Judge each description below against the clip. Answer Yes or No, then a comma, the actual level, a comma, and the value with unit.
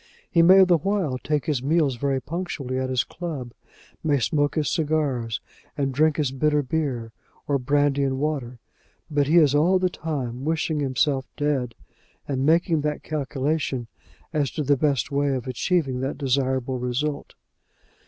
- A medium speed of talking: Yes, average, 160 wpm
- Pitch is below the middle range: No, medium, 145 Hz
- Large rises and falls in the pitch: No, average, 3.0 semitones